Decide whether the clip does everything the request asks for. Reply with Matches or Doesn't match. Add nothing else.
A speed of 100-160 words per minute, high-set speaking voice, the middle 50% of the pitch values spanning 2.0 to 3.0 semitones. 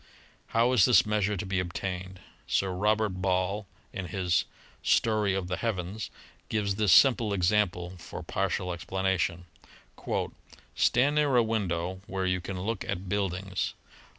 Doesn't match